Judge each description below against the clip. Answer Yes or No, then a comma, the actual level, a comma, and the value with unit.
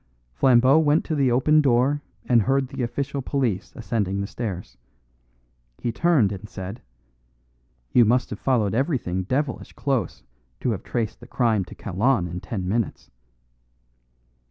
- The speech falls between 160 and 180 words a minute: No, average, 145 wpm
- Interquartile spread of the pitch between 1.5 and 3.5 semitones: No, average, 4.9 semitones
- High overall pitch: No, low, 120 Hz